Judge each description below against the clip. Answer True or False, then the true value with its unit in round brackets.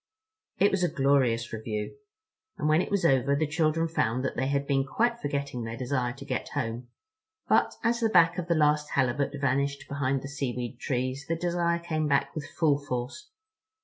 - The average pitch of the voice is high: False (140 Hz)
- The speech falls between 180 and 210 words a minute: True (190 wpm)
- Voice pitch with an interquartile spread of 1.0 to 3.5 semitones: False (3.9 semitones)